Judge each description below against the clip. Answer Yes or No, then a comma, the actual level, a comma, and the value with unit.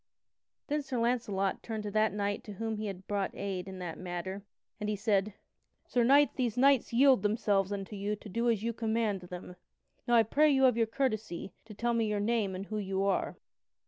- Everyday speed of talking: No, fast, 210 wpm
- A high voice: Yes, high, 215 Hz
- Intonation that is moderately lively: Yes, average, 3.0 semitones